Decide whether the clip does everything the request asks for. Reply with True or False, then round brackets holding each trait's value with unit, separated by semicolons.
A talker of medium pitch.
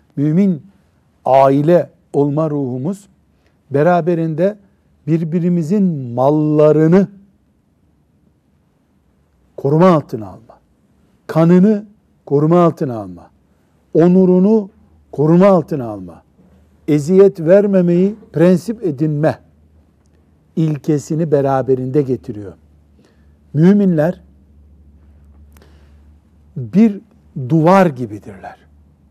True (145 Hz)